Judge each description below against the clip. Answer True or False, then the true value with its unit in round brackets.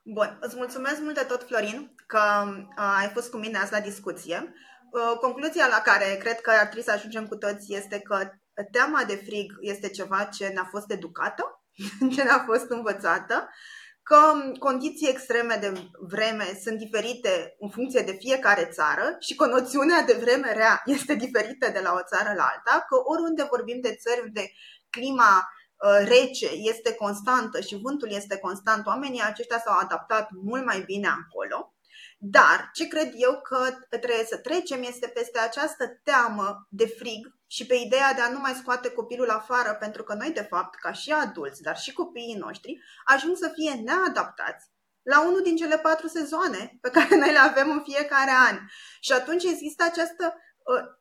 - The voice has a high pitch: True (245 Hz)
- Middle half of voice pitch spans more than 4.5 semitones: True (4.9 semitones)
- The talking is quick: True (175 wpm)